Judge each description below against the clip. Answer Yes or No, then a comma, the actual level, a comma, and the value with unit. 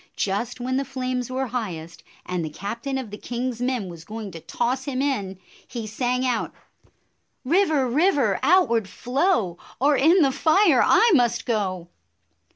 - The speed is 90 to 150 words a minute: No, average, 170 wpm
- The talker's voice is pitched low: No, high, 245 Hz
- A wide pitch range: No, average, 4.6 semitones